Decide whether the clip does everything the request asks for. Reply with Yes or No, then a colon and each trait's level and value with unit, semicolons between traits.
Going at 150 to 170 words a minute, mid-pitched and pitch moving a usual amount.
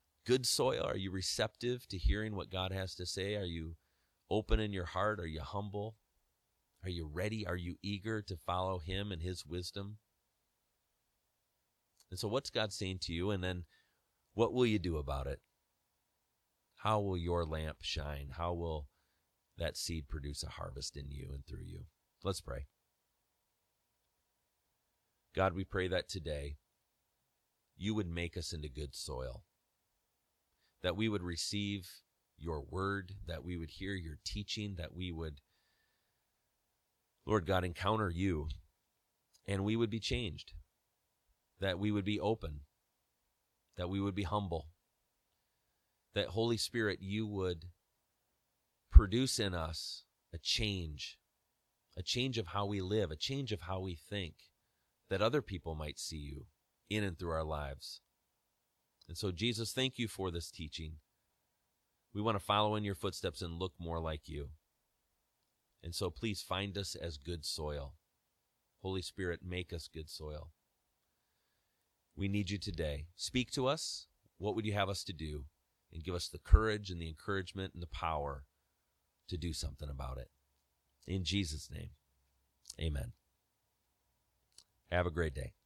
No: average, 155 wpm; very low, 90 Hz; average, 4.5 semitones